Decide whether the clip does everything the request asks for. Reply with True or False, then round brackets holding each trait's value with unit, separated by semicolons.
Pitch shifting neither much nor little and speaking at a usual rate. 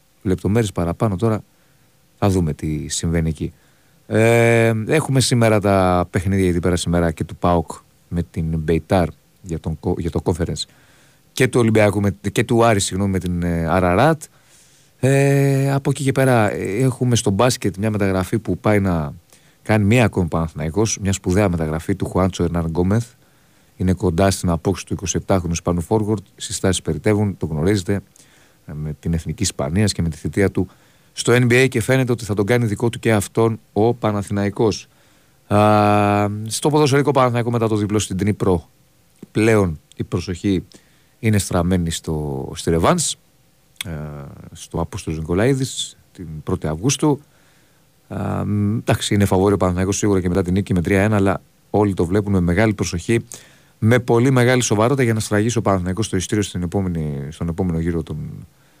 True (4.7 semitones; 155 wpm)